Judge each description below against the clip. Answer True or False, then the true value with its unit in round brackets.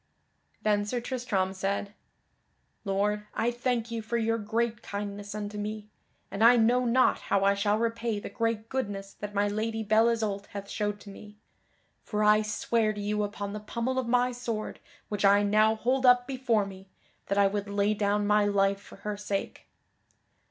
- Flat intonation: True (2.2 semitones)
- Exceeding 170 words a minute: True (180 wpm)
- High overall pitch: True (210 Hz)